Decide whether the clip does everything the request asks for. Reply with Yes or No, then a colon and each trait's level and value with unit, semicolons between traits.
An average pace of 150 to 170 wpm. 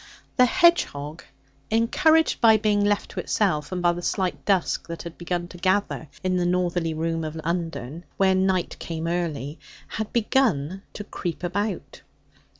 Yes: average, 155 wpm